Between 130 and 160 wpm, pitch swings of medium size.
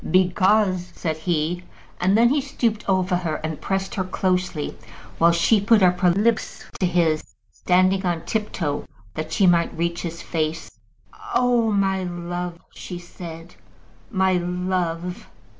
No: average, 155 wpm; narrow, 2.2 semitones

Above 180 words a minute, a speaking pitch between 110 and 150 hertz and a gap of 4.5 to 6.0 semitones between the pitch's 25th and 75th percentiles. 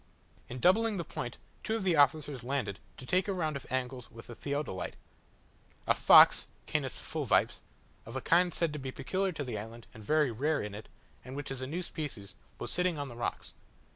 Yes: fast, 205 wpm; medium, 140 Hz; average, 5.3 semitones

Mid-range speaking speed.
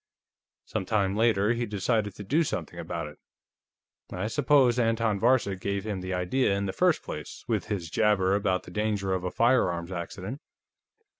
Yes: average, 170 wpm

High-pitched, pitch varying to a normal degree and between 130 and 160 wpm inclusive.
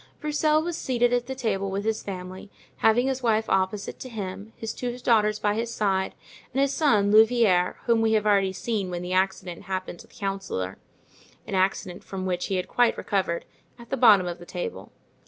No: high, 205 Hz; average, 3.9 semitones; average, 190 wpm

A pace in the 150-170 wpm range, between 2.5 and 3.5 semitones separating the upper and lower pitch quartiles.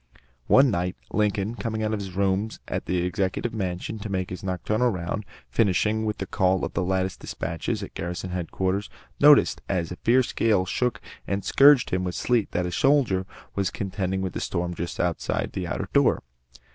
No: average, 190 wpm; average, 3.2 semitones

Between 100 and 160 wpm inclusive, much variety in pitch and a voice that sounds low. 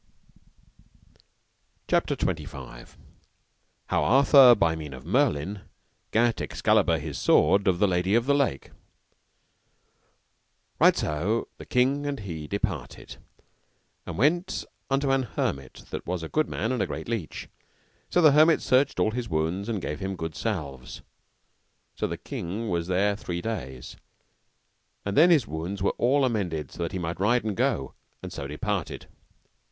Yes: average, 150 wpm; wide, 7.2 semitones; low, 100 Hz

